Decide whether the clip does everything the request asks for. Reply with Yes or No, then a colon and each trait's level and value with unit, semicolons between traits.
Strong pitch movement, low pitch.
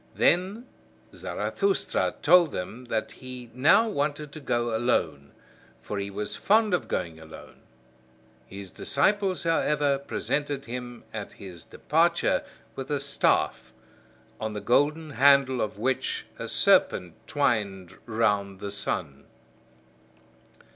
Yes: wide, 6.5 semitones; low, 125 Hz